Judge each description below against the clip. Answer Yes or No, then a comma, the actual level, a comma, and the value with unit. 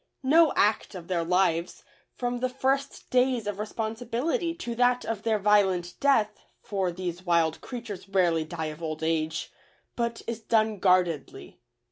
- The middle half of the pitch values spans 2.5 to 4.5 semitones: No, wide, 5.6 semitones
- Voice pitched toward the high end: Yes, high, 210 Hz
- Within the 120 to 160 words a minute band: Yes, average, 150 wpm